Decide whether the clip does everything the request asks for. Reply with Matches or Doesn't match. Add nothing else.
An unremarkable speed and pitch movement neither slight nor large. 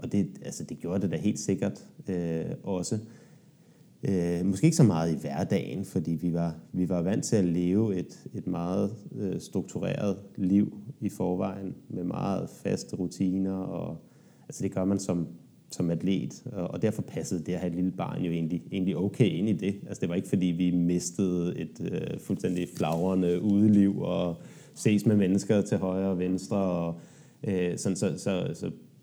Doesn't match